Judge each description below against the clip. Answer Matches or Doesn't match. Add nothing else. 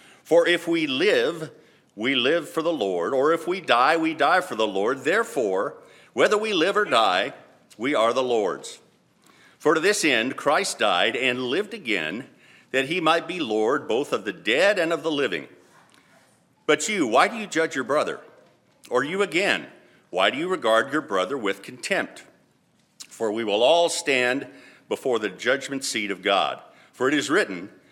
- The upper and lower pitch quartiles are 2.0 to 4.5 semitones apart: Doesn't match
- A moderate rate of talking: Matches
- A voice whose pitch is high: Doesn't match